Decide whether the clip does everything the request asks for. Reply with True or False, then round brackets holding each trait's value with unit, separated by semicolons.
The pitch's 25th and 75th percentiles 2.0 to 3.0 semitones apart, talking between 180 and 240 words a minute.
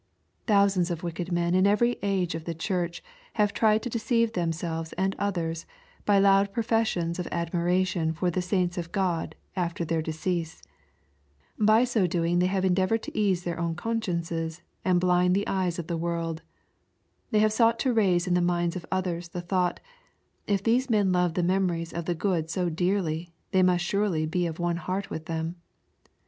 True (2.6 semitones; 190 wpm)